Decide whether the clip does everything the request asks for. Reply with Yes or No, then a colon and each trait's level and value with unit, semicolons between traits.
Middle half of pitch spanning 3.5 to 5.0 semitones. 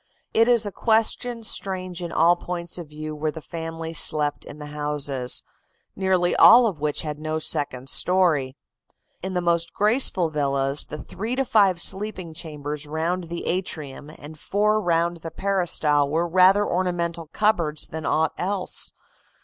Yes: average, 3.8 semitones